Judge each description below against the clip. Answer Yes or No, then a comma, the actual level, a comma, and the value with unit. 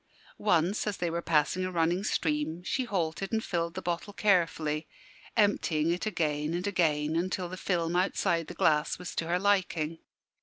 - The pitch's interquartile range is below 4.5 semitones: Yes, narrow, 2.6 semitones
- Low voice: No, medium, 175 Hz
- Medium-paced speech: Yes, average, 175 wpm